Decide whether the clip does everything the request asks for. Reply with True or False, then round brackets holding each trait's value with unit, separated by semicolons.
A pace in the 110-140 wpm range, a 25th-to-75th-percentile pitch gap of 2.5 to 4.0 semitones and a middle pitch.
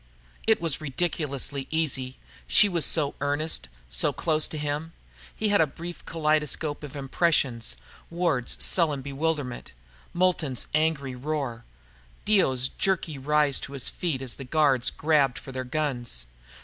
True (135 wpm; 3.4 semitones; 145 Hz)